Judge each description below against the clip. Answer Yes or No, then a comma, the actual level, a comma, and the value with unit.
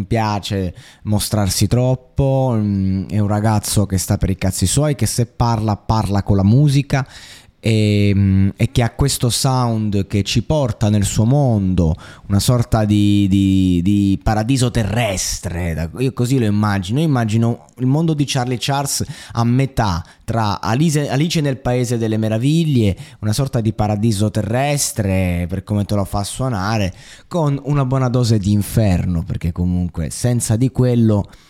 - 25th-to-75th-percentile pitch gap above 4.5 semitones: No, average, 4.1 semitones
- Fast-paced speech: No, average, 150 wpm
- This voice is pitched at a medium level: No, low, 110 Hz